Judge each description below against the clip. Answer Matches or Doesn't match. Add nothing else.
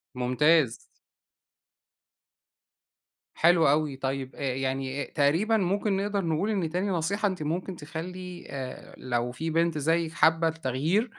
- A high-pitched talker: Doesn't match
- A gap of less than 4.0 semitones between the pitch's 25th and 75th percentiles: Doesn't match